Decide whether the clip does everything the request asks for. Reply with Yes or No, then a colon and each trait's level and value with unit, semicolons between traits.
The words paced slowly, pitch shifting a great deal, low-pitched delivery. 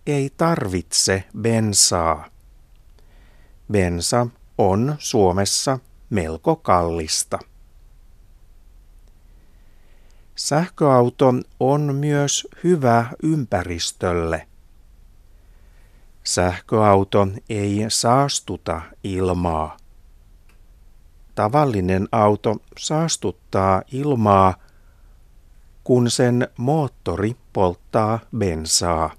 Yes: slow, 55 wpm; wide, 6.0 semitones; low, 100 Hz